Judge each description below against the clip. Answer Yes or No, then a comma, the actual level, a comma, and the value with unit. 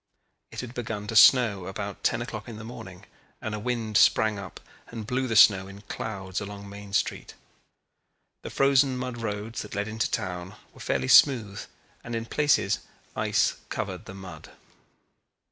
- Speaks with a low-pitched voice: Yes, low, 110 Hz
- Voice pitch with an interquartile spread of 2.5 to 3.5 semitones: Yes, average, 2.9 semitones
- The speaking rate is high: No, average, 165 wpm